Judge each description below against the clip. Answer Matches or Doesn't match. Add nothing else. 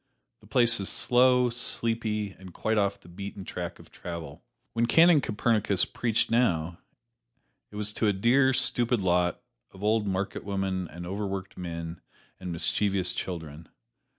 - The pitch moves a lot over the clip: Doesn't match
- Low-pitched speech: Matches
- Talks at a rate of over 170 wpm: Doesn't match